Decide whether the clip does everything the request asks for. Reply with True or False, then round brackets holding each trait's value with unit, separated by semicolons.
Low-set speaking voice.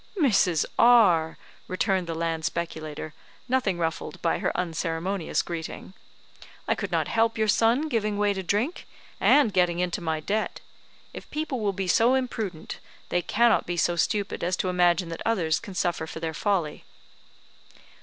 False (185 Hz)